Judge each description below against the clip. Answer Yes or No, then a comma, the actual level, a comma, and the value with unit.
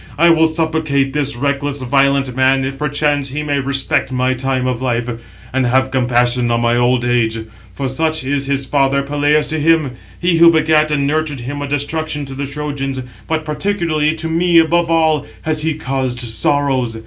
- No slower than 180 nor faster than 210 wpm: Yes, average, 185 wpm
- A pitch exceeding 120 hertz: Yes, medium, 140 Hz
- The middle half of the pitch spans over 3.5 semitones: No, average, 3.0 semitones